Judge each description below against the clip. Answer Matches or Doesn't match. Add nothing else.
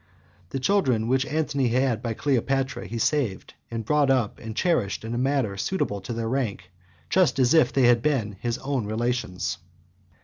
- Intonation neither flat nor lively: Matches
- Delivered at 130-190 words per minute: Matches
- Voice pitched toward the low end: Matches